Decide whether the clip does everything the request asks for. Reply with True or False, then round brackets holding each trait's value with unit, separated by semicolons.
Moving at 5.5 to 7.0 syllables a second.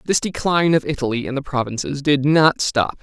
True (5.6 syllables/s)